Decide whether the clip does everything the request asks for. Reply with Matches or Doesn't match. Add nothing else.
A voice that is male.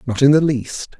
Matches